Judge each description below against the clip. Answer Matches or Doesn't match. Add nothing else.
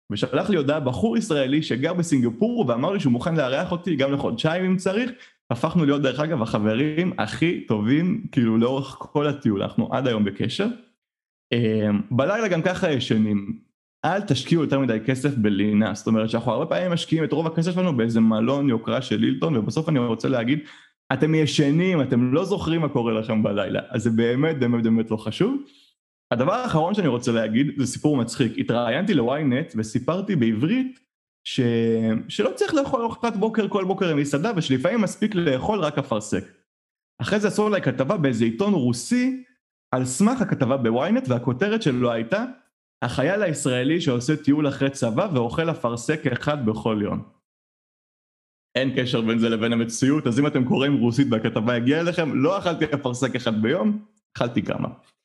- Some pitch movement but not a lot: Doesn't match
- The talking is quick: Matches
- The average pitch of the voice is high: Doesn't match